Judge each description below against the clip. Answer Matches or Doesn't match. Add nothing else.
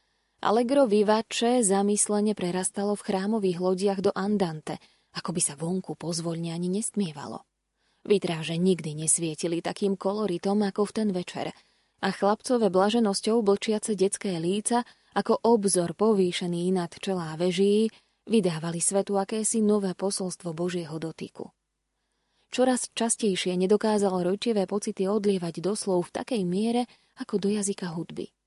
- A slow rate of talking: Doesn't match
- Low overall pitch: Doesn't match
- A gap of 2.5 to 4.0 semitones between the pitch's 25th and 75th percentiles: Matches